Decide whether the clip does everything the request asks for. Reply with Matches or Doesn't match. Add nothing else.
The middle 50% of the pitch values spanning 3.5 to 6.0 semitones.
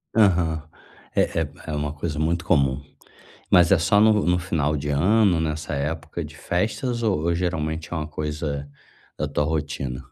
Doesn't match